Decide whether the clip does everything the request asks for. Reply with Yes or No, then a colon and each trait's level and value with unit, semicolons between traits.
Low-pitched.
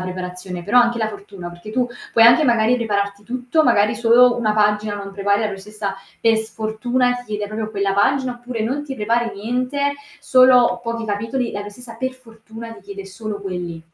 No: high, 220 Hz